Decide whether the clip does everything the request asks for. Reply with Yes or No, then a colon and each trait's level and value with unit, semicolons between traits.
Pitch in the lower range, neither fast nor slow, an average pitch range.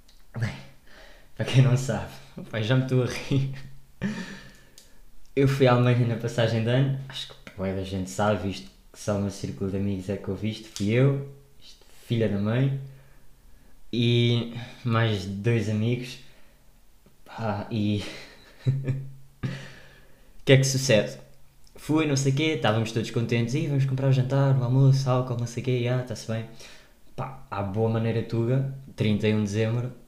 Yes: low, 120 Hz; average, 160 wpm; average, 3.8 semitones